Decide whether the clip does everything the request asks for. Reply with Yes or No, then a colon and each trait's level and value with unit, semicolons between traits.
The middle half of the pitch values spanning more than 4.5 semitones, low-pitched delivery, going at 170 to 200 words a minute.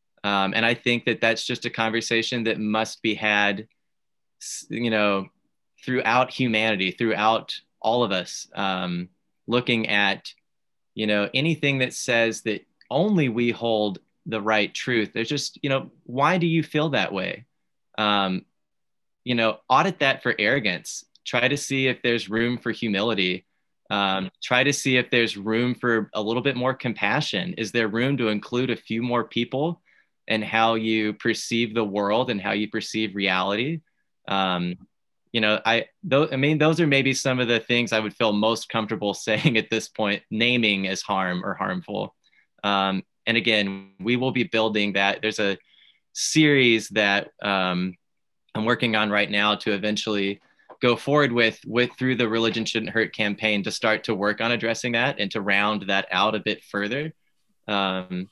No: average, 3.1 semitones; low, 110 Hz; average, 175 wpm